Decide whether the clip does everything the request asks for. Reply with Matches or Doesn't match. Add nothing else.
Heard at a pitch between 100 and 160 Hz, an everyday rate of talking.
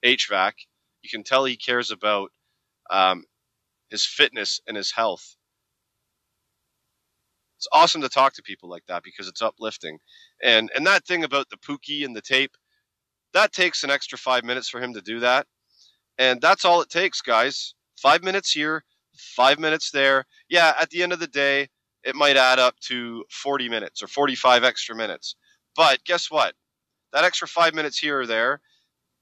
Matches